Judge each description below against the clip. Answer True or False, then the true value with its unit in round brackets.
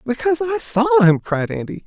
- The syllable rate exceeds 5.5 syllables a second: True (5.7 syllables/s)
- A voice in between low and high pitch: False (220 Hz)